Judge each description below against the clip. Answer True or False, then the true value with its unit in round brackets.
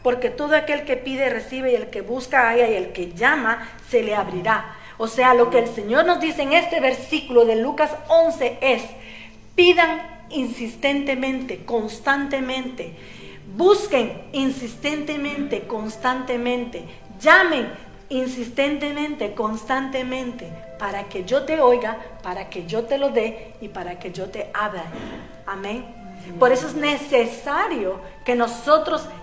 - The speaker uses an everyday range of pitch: True (4.0 semitones)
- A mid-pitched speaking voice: False (250 Hz)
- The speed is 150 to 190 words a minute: False (135 wpm)